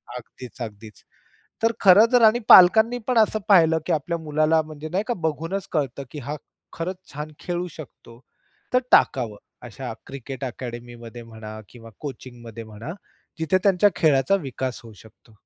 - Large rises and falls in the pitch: Yes, wide, 7.0 semitones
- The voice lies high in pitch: No, medium, 150 Hz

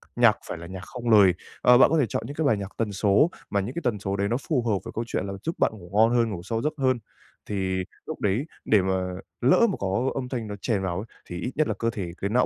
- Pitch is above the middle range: No, low, 110 Hz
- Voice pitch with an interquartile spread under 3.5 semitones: No, average, 4.3 semitones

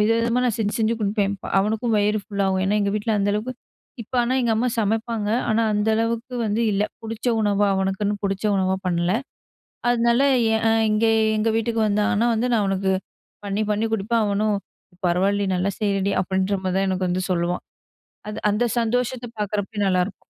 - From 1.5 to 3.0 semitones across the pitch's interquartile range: Yes, narrow, 2.4 semitones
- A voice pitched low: No, high, 210 Hz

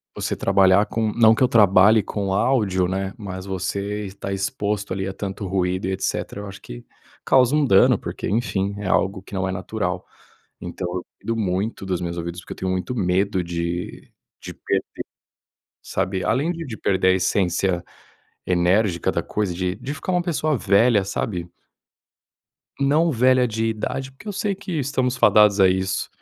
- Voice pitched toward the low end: Yes, low, 100 Hz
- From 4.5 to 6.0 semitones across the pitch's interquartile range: No, average, 3.4 semitones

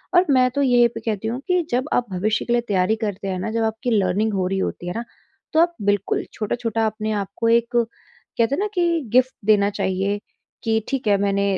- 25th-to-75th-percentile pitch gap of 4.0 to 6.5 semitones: No, average, 3.4 semitones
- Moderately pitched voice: No, high, 220 Hz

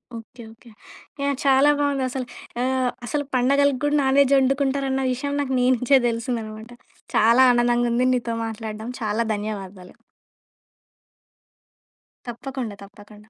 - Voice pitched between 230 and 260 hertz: Yes, very high, 250 Hz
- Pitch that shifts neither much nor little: Yes, average, 3.1 semitones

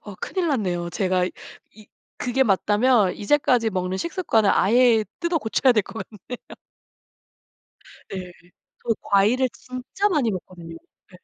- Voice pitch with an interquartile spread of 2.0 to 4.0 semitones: No, average, 5.1 semitones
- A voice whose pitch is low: No, high, 220 Hz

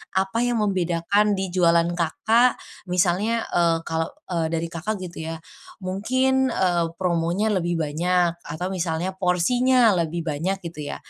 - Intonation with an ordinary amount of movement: Yes, average, 3.4 semitones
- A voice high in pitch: No, medium, 180 Hz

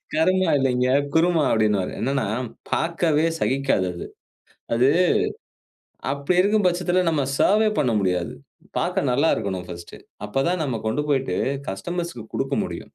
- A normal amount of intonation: No, wide, 7.2 semitones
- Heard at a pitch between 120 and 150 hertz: Yes, medium, 140 Hz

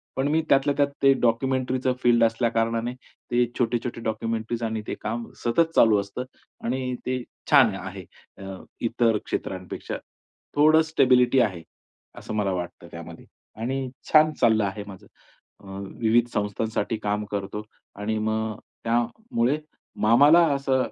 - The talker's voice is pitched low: Yes, low, 115 Hz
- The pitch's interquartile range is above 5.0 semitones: No, average, 3.2 semitones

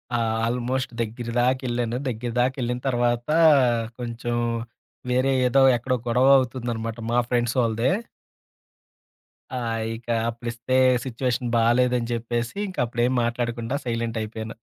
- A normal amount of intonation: No, narrow, 1.2 semitones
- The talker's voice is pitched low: Yes, low, 120 Hz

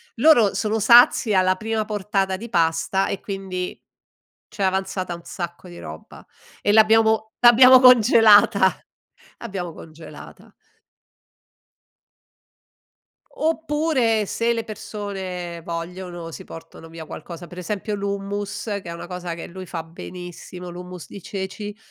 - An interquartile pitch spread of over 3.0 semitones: Yes, average, 3.6 semitones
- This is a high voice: Yes, high, 195 Hz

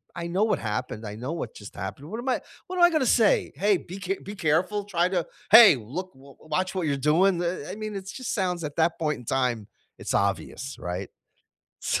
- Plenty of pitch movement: Yes, wide, 7.1 semitones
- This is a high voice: No, medium, 170 Hz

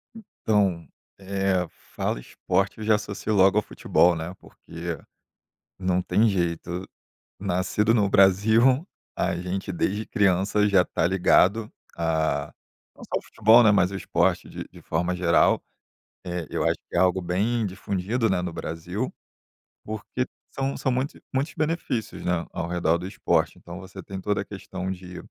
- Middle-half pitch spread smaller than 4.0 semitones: Yes, average, 3.1 semitones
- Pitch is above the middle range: No, very low, 95 Hz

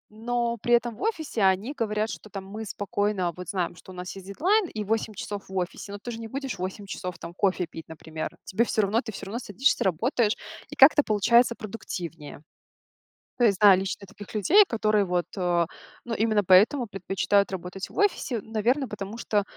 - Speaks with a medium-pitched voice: No, high, 210 Hz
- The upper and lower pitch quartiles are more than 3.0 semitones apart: Yes, average, 3.7 semitones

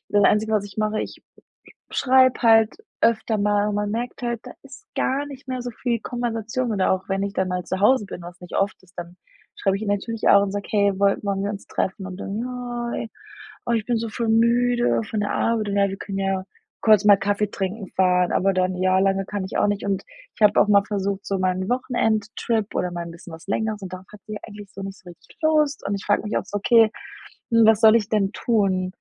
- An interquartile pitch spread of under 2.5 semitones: No, average, 2.8 semitones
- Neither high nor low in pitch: No, high, 205 Hz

